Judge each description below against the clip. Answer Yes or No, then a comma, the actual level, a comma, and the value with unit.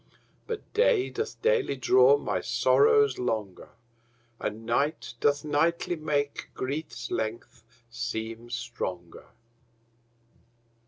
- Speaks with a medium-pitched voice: Yes, medium, 145 Hz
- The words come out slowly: Yes, slow, 95 wpm